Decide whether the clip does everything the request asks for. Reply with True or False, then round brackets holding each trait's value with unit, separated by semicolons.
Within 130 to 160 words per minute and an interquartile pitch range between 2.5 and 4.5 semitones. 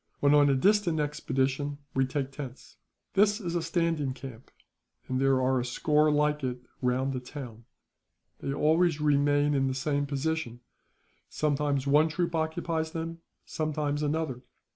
True (150 wpm; 3.1 semitones)